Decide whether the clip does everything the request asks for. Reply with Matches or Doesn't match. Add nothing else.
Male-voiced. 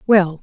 Doesn't match